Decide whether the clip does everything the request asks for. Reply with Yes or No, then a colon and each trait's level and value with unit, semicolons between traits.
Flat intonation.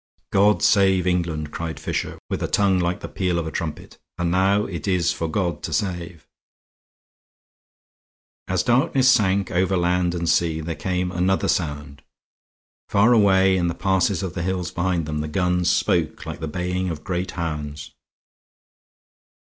Yes: narrow, 2.2 semitones